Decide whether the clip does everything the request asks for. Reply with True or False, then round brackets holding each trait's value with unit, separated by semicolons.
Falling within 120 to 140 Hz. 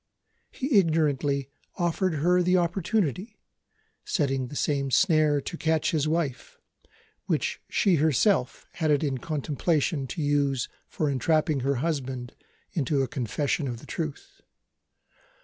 False (150 Hz)